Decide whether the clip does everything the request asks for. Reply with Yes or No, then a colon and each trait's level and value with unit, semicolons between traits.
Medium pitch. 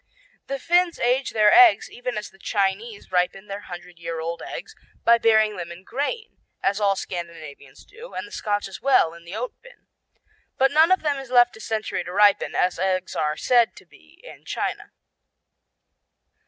No: high, 210 Hz